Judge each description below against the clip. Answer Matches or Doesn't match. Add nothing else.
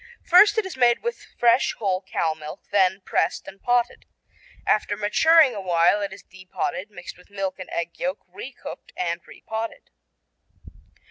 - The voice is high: Matches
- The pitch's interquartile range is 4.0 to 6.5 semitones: Matches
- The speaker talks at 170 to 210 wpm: Matches